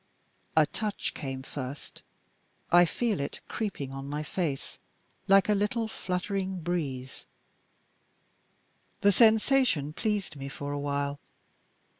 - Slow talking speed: Yes, slow, 115 wpm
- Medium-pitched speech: Yes, medium, 175 Hz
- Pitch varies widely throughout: Yes, wide, 6.3 semitones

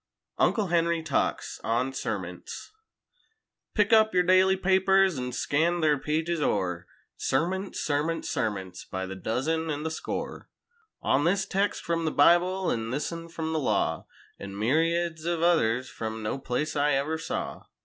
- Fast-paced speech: No, average, 155 wpm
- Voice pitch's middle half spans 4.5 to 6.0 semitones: Yes, average, 5.1 semitones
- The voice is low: No, medium, 160 Hz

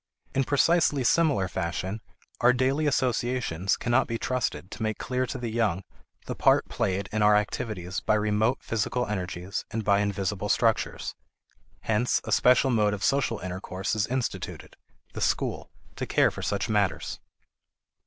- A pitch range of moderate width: Yes, average, 4.0 semitones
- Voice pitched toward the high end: No, low, 110 Hz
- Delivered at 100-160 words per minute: Yes, average, 155 wpm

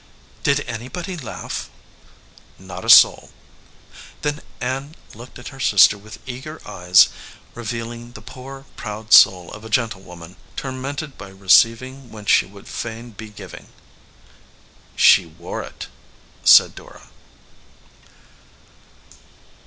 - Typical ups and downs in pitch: Yes, average, 4.3 semitones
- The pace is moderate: No, slow, 115 wpm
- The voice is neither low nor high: No, low, 115 Hz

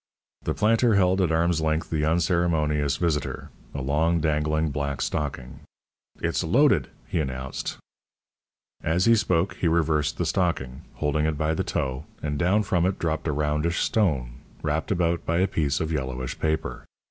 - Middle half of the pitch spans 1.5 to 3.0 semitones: Yes, average, 2.7 semitones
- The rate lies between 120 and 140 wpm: No, average, 160 wpm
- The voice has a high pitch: No, very low, 80 Hz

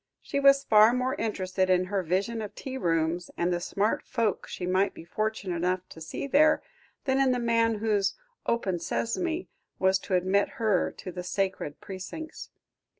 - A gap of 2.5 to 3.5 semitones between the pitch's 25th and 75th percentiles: No, average, 4.3 semitones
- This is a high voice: Yes, high, 200 Hz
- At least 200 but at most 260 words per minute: No, average, 175 wpm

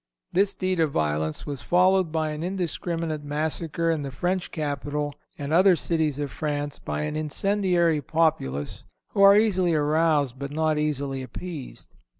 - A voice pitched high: No, medium, 155 Hz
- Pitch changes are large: No, average, 3.2 semitones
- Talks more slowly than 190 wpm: Yes, average, 155 wpm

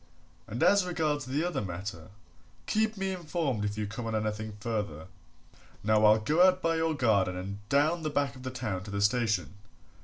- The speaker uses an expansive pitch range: Yes, wide, 7.3 semitones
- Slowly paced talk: No, average, 190 wpm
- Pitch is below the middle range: Yes, low, 120 Hz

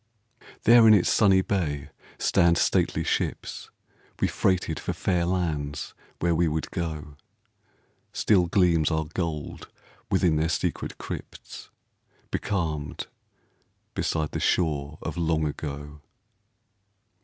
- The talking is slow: Yes, slow, 110 wpm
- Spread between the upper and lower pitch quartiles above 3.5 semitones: No, average, 2.9 semitones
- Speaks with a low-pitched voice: Yes, very low, 80 Hz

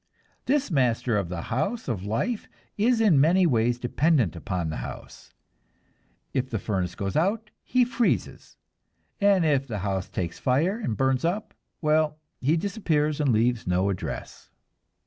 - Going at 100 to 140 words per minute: No, average, 150 wpm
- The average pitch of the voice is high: No, low, 135 Hz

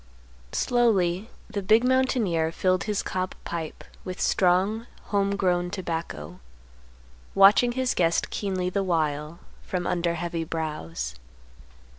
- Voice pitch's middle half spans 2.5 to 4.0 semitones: Yes, average, 3.4 semitones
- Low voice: No, medium, 185 Hz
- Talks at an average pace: No, slow, 115 wpm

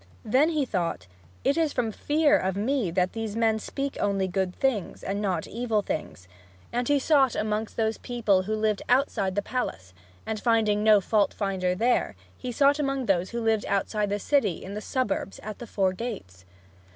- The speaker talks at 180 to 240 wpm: Yes, average, 190 wpm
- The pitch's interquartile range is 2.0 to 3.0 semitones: No, average, 4.1 semitones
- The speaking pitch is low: No, high, 215 Hz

